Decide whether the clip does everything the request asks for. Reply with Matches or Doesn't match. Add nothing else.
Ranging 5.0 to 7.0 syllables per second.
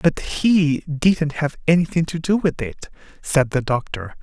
Doesn't match